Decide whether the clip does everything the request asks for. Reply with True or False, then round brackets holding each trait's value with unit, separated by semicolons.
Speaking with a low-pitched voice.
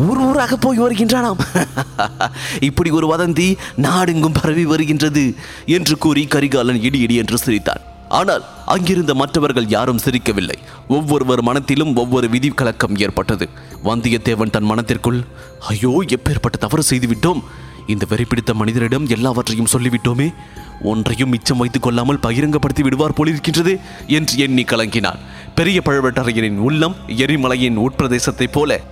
True (130 Hz)